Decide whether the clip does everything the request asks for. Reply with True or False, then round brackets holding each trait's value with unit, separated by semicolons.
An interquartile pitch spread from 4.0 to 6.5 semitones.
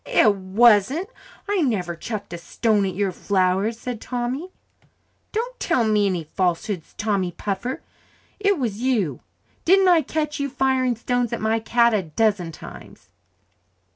True (5.1 semitones)